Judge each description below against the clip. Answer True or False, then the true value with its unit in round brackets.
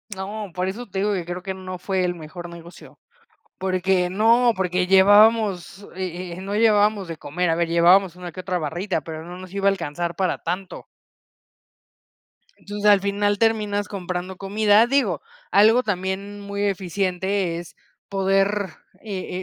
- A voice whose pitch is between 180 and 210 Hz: True (190 Hz)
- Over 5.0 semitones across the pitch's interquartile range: False (2.4 semitones)